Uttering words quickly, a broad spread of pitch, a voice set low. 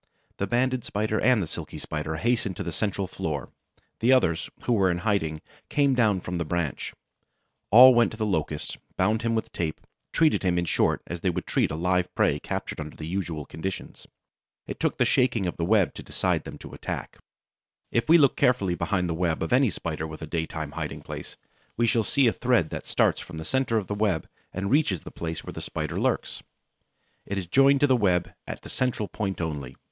Yes: fast, 215 wpm; wide, 6.0 semitones; very low, 95 Hz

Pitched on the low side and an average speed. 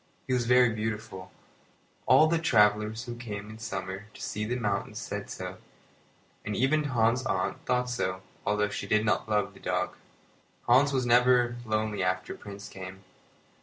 Yes: low, 110 Hz; average, 165 wpm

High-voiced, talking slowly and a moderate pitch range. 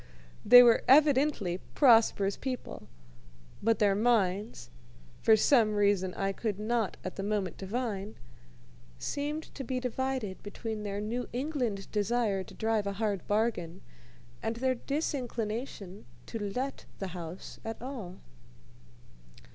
Yes: high, 220 Hz; slow, 125 wpm; average, 3.9 semitones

